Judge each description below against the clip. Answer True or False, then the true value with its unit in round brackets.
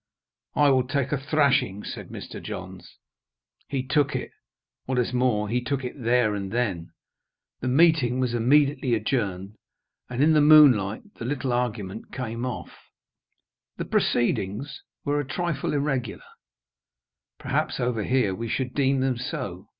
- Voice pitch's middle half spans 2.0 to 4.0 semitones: True (3.2 semitones)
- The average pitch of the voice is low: True (125 Hz)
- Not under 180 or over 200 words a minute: False (145 wpm)